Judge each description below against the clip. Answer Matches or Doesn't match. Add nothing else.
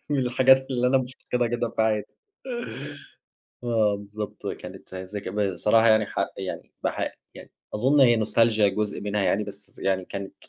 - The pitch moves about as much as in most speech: Matches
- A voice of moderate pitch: Doesn't match